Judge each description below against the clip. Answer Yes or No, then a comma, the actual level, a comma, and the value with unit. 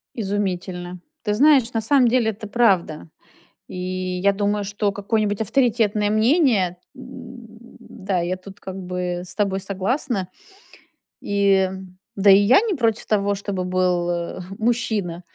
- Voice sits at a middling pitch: No, high, 205 Hz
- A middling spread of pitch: Yes, average, 3.5 semitones